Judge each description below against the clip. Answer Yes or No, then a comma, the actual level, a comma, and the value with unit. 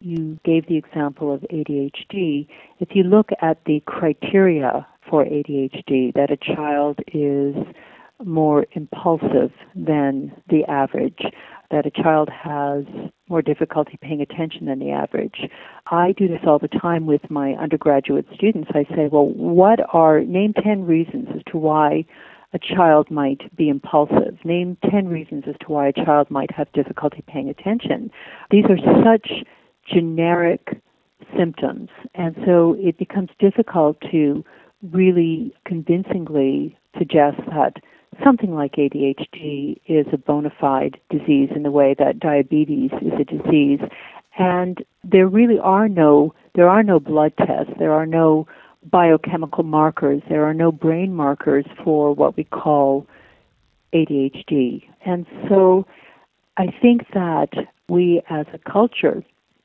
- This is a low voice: No, medium, 155 Hz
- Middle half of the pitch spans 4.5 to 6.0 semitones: No, average, 3.8 semitones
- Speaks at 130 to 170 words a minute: Yes, average, 140 wpm